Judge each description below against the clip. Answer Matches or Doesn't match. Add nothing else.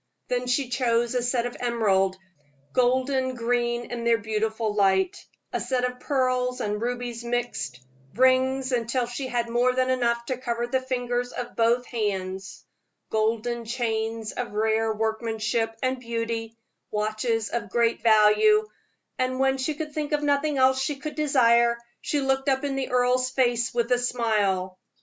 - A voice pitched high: Matches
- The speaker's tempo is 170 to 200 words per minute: Doesn't match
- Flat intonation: Matches